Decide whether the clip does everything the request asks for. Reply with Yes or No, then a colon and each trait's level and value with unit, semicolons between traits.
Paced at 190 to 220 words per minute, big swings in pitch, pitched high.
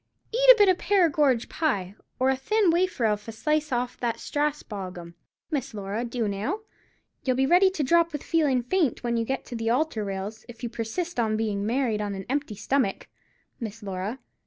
Yes: average, 200 wpm; wide, 6.0 semitones; high, 245 Hz